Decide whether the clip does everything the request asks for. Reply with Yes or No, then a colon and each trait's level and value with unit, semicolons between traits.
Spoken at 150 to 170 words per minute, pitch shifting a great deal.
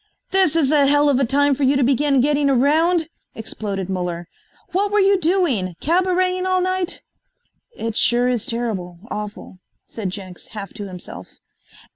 Yes: average, 160 wpm; wide, 8.4 semitones